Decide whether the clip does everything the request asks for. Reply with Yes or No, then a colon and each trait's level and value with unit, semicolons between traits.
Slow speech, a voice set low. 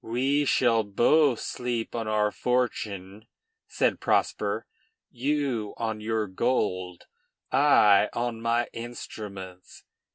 Yes: slow, 100 wpm; low, 115 Hz